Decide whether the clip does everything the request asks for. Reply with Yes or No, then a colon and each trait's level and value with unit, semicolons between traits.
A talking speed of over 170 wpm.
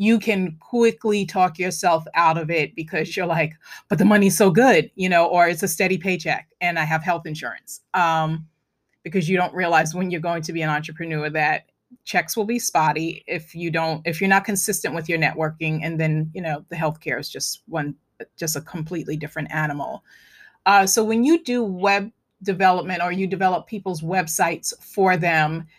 Yes: average, 195 wpm